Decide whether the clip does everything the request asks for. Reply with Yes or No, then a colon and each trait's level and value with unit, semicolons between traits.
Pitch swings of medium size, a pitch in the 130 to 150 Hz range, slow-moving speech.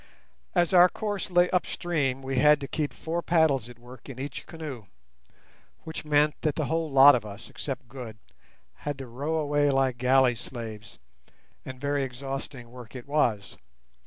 No: average, 3.5 semitones; low, 135 Hz; average, 165 wpm